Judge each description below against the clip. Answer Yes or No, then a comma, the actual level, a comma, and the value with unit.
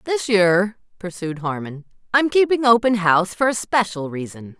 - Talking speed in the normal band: Yes, average, 155 wpm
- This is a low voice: No, high, 200 Hz